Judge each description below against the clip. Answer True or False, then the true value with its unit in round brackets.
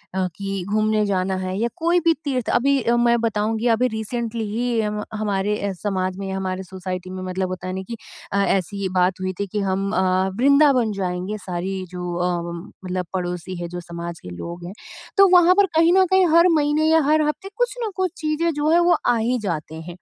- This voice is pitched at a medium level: False (205 Hz)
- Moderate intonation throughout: False (5.9 semitones)